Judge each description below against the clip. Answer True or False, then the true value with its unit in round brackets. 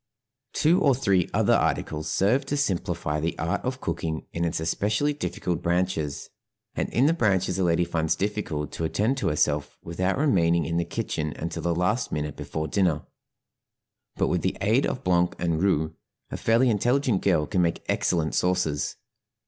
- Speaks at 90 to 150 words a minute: False (175 wpm)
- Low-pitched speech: True (90 Hz)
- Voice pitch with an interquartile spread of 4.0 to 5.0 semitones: True (4.6 semitones)